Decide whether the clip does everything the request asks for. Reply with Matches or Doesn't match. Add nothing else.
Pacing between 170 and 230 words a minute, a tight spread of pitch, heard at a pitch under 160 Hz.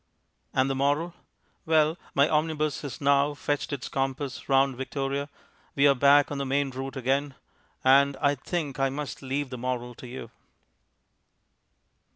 Doesn't match